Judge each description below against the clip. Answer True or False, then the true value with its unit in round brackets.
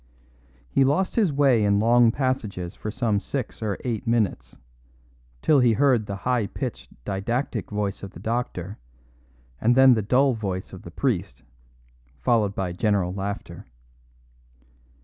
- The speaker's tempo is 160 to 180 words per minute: False (145 wpm)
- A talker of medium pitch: False (110 Hz)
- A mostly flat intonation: False (4.1 semitones)